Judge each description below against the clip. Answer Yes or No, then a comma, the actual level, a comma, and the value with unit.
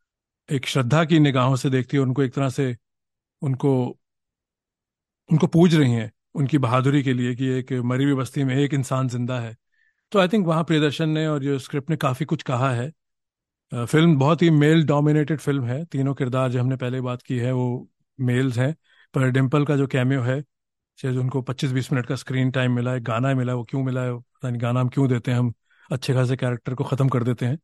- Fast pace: Yes, fast, 215 wpm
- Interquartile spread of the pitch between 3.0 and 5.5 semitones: No, narrow, 2.6 semitones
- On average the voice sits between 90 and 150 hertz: Yes, low, 135 Hz